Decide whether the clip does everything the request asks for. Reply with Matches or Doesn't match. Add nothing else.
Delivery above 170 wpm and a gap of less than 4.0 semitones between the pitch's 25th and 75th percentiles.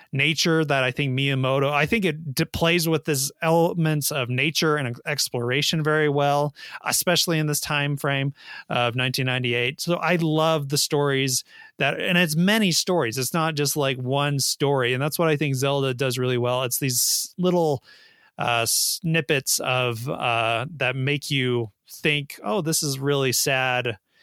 Doesn't match